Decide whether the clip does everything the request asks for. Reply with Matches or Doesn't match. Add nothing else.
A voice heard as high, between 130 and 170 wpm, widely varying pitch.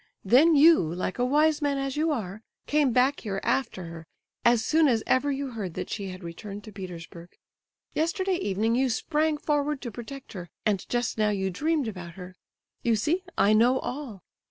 Doesn't match